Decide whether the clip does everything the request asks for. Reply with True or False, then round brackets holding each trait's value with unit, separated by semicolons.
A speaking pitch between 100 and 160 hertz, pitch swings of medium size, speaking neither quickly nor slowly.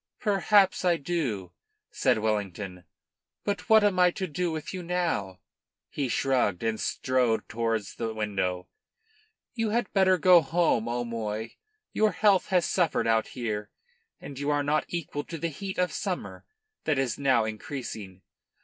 False (140 Hz; 8.4 semitones; 150 wpm)